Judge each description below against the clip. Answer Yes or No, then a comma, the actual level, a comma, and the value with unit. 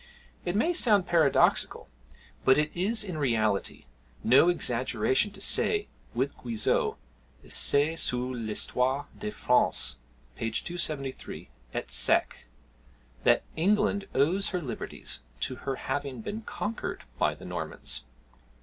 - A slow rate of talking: Yes, slow, 120 wpm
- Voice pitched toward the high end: No, medium, 140 Hz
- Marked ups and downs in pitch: Yes, wide, 7.0 semitones